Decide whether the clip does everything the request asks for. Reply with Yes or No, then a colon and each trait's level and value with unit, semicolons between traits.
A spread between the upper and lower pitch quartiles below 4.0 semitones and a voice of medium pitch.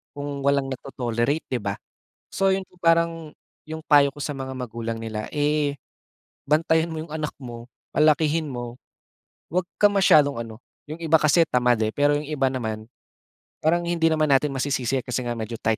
No: average, 4.4 semitones; medium, 145 Hz